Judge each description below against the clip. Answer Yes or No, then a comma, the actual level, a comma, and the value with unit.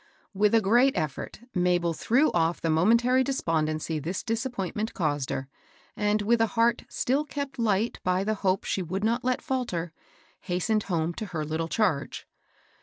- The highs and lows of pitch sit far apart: Yes, wide, 5.8 semitones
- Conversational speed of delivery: Yes, average, 170 wpm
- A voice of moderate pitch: No, high, 200 Hz